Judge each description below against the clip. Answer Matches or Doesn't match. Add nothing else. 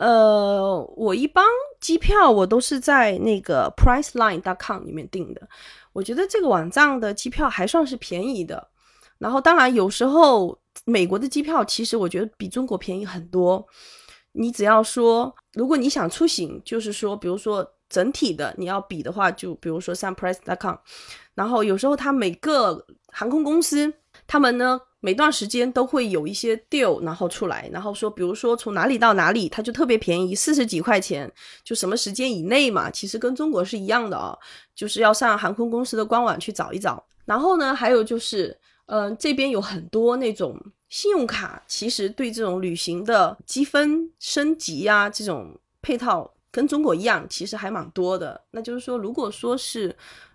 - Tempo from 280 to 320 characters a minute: Matches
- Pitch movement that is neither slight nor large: Doesn't match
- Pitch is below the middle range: Doesn't match